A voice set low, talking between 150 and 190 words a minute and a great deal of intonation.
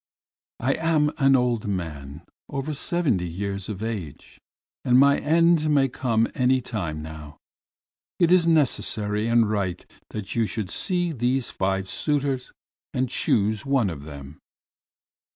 No: low, 115 Hz; slow, 135 wpm; wide, 6.5 semitones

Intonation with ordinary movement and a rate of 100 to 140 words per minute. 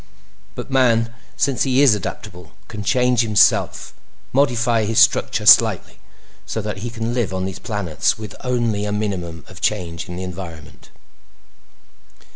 Yes: average, 4.4 semitones; slow, 135 wpm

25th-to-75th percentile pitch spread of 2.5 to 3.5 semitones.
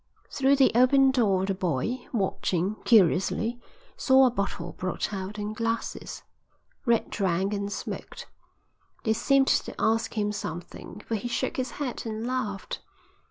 No: average, 4.2 semitones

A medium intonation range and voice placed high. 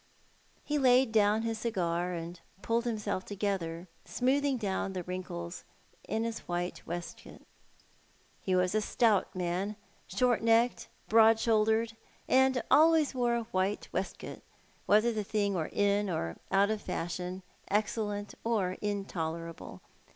Yes: average, 3.9 semitones; high, 205 Hz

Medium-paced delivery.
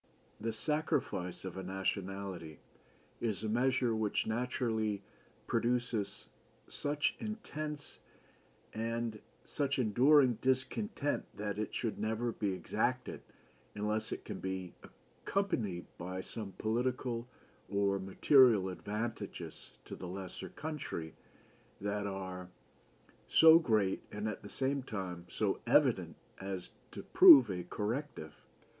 No: slow, 115 wpm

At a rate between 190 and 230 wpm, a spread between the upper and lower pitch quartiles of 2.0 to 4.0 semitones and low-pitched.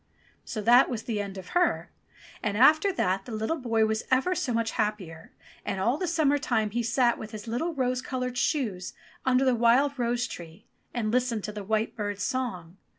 No: average, 200 wpm; average, 3.5 semitones; high, 235 Hz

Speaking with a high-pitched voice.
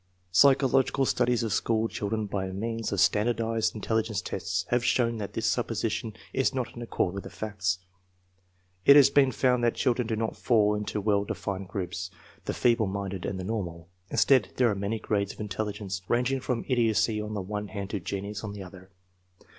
No: low, 105 Hz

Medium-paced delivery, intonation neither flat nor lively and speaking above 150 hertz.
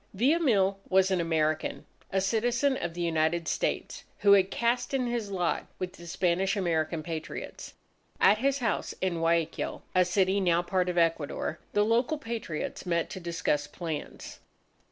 Yes: average, 160 wpm; average, 4.0 semitones; medium, 185 Hz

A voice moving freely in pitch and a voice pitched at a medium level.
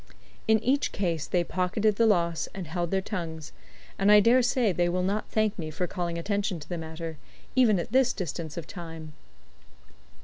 No: average, 4.0 semitones; medium, 180 Hz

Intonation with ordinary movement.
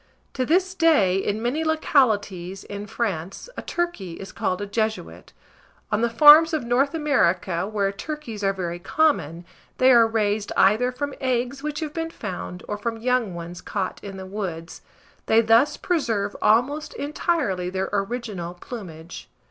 No: wide, 6.5 semitones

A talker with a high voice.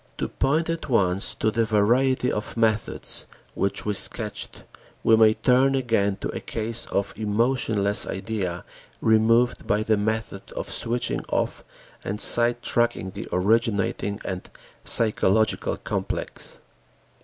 No: low, 110 Hz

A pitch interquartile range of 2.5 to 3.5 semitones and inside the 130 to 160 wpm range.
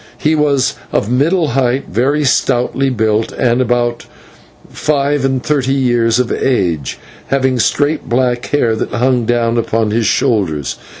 Yes: average, 2.8 semitones; average, 140 wpm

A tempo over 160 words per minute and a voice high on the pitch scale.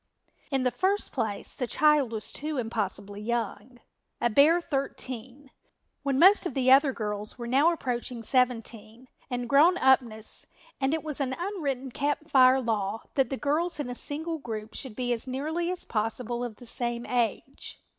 Yes: average, 175 wpm; very high, 255 Hz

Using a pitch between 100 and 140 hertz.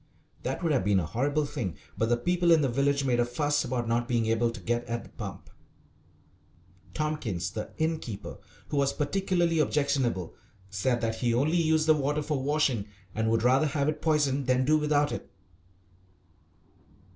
Yes: low, 135 Hz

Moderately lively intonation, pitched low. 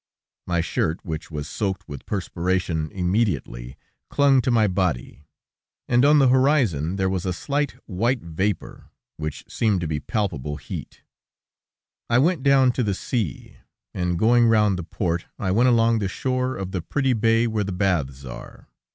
No: wide, 6.1 semitones; very low, 95 Hz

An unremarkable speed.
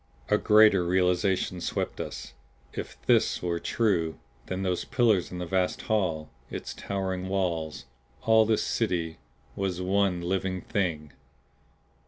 No: slow, 130 wpm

